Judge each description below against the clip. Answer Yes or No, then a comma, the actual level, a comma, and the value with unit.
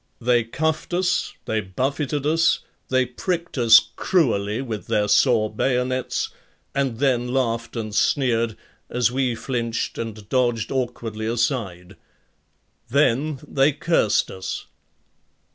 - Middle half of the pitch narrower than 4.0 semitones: Yes, average, 3.2 semitones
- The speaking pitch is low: Yes, low, 120 Hz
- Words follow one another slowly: Yes, slow, 115 wpm